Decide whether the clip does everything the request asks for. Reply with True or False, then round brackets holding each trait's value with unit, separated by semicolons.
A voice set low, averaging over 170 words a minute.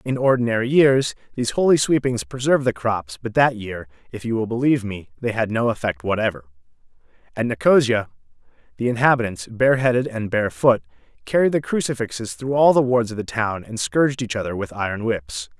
True (115 Hz; 185 wpm)